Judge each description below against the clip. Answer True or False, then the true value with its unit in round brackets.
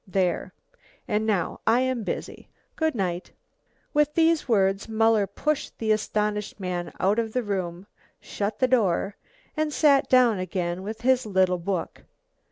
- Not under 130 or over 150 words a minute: True (145 wpm)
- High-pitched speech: True (210 Hz)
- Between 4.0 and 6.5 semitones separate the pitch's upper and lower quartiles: True (5.0 semitones)